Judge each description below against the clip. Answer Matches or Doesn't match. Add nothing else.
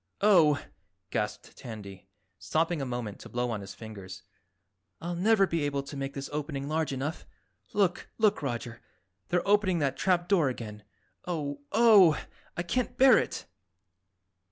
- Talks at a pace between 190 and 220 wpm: Doesn't match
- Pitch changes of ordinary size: Doesn't match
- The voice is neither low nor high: Matches